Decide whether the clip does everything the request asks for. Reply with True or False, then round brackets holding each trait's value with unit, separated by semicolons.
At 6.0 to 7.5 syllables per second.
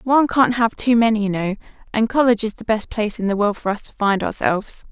True (6.5 syllables/s)